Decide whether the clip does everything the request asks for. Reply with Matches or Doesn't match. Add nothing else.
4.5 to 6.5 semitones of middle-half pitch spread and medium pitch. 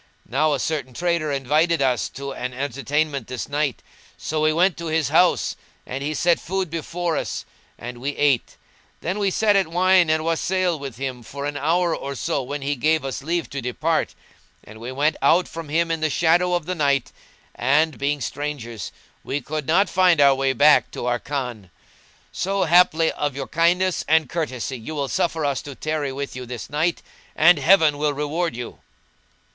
Doesn't match